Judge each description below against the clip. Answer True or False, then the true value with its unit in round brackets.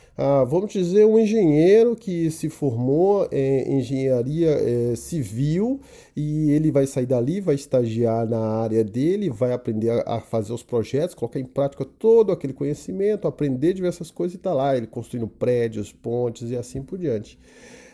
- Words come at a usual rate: True (160 wpm)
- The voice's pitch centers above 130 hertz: True (140 Hz)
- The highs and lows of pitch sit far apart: True (6.0 semitones)